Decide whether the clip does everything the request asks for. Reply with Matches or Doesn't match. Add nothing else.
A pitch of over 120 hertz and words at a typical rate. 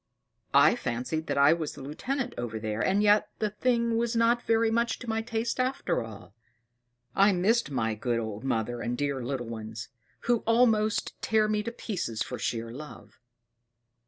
Matches